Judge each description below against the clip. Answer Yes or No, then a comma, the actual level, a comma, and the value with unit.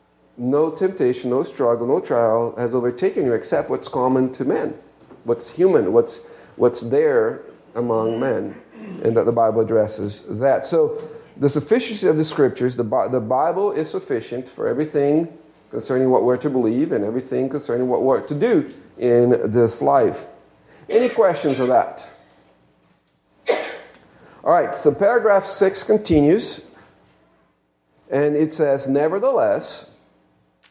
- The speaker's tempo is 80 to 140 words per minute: Yes, slow, 135 wpm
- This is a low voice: Yes, low, 130 Hz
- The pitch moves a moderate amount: No, wide, 7.2 semitones